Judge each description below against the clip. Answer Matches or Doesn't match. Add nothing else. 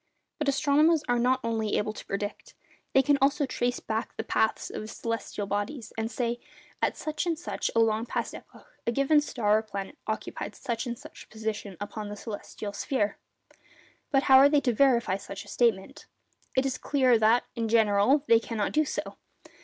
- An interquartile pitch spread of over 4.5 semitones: Doesn't match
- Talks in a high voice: Matches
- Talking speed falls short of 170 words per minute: Doesn't match